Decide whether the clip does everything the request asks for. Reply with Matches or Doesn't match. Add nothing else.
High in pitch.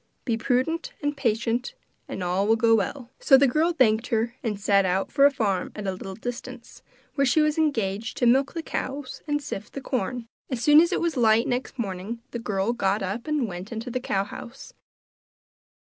Matches